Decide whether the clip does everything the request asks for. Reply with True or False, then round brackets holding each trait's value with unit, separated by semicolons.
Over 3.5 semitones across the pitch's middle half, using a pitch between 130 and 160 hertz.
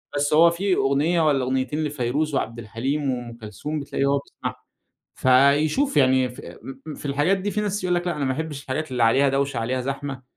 False (3.2 semitones; 140 Hz)